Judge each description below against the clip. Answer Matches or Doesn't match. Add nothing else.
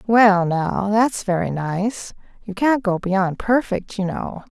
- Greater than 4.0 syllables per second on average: Doesn't match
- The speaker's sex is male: Doesn't match